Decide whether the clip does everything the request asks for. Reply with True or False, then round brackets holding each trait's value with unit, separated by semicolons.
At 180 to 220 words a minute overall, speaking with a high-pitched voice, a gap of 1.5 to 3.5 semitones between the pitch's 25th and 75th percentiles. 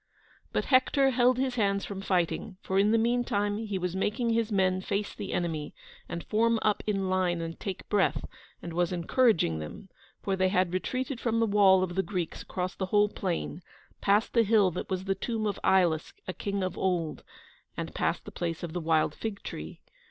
True (200 wpm; 195 Hz; 3.2 semitones)